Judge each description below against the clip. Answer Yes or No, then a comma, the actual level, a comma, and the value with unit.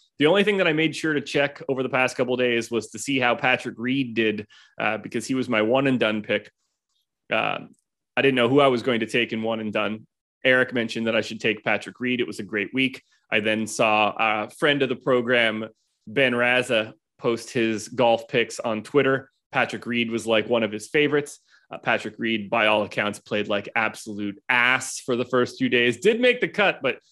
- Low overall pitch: Yes, low, 120 Hz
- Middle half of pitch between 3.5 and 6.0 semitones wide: No, average, 3.1 semitones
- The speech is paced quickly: Yes, fast, 225 wpm